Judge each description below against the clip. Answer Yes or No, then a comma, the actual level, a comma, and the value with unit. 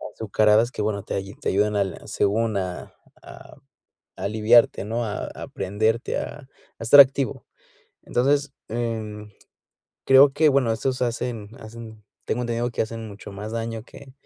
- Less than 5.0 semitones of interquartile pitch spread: Yes, narrow, 2.6 semitones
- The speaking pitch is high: No, low, 115 Hz